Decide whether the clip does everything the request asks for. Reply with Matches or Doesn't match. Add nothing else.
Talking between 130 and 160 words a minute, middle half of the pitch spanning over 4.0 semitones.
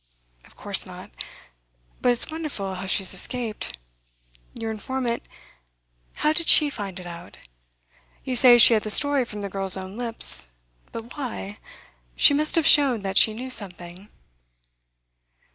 Matches